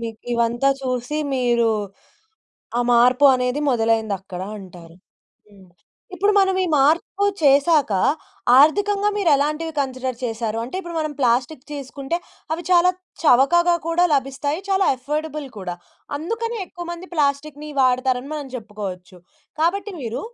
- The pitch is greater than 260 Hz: Yes, very high, 275 Hz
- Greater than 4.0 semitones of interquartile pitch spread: Yes, wide, 5.5 semitones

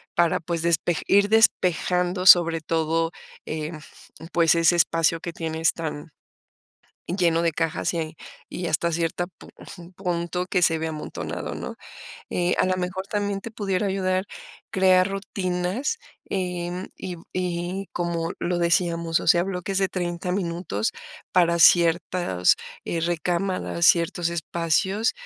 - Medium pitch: Yes, medium, 175 Hz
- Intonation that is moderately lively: No, narrow, 1.9 semitones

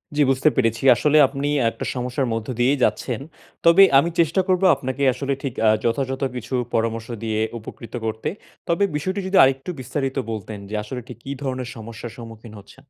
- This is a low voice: Yes, low, 130 Hz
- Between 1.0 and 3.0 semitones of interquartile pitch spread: No, average, 3.7 semitones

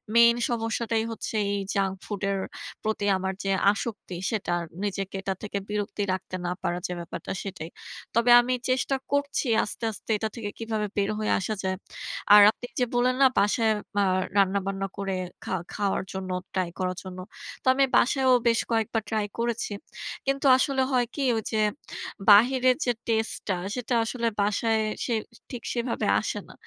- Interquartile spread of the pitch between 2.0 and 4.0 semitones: Yes, average, 3.4 semitones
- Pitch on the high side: Yes, high, 220 Hz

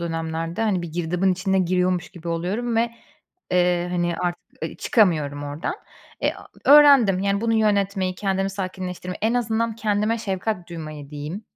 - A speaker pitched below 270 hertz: Yes, medium, 185 Hz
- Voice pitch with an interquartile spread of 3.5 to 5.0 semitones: Yes, average, 3.8 semitones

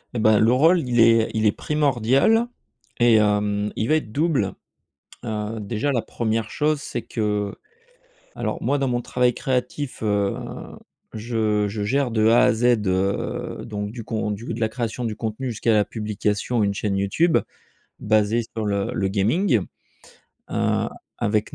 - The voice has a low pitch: Yes, low, 110 Hz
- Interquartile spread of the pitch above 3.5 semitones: No, average, 2.9 semitones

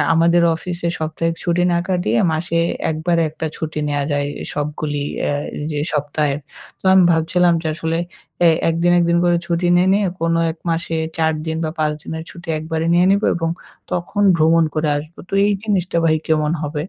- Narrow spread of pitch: Yes, narrow, 1.8 semitones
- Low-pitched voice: No, medium, 165 Hz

